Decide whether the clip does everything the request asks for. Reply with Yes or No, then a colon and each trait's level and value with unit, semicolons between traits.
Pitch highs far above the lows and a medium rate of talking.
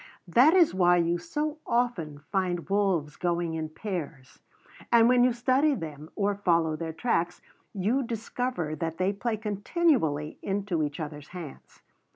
Yes: wide, 6.5 semitones; average, 150 wpm